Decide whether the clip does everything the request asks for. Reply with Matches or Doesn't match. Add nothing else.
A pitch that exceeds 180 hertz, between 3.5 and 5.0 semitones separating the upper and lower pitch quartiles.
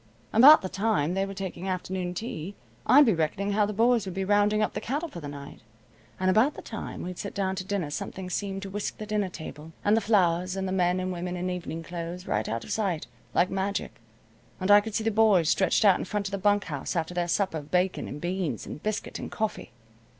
Doesn't match